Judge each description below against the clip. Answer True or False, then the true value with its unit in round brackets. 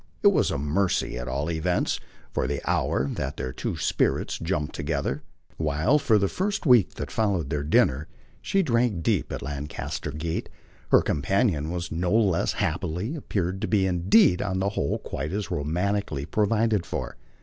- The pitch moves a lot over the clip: True (5.7 semitones)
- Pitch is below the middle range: True (90 Hz)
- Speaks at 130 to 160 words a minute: False (170 wpm)